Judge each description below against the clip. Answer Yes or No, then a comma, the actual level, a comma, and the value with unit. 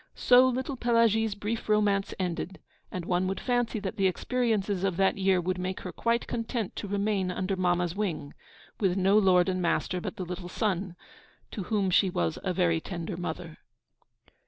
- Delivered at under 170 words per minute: No, average, 180 wpm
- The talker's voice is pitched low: No, high, 190 Hz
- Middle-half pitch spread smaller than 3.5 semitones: Yes, average, 2.9 semitones